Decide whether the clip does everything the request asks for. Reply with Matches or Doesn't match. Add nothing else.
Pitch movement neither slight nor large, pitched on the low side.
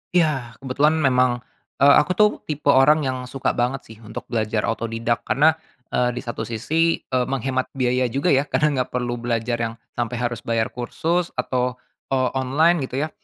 Matches